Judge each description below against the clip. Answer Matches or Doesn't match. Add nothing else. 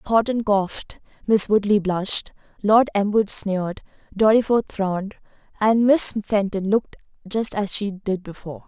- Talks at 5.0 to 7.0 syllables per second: Doesn't match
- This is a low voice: Doesn't match